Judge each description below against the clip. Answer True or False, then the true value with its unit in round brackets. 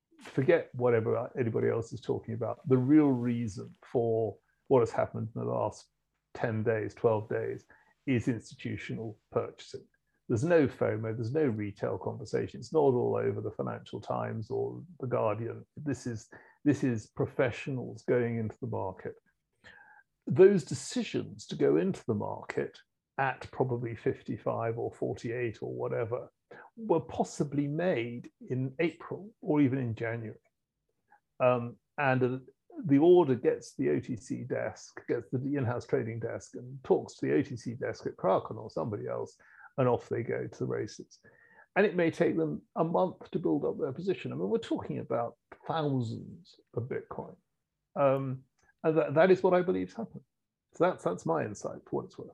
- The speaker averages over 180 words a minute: False (170 wpm)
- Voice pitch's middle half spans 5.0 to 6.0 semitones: True (5.6 semitones)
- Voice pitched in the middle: False (130 Hz)